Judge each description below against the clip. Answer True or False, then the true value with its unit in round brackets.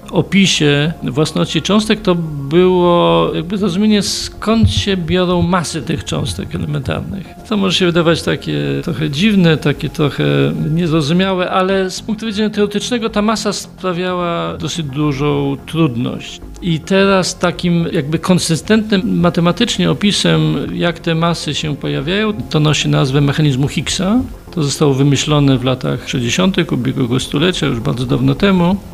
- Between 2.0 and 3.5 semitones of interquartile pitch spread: False (4.3 semitones)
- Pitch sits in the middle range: True (170 Hz)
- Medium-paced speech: True (135 wpm)